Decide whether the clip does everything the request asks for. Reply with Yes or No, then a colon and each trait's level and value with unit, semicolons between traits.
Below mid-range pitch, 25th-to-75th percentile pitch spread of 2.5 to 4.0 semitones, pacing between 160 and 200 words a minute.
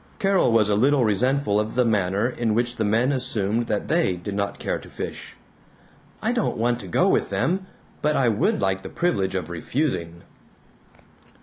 No: low, 110 Hz; average, 4.4 semitones; average, 185 wpm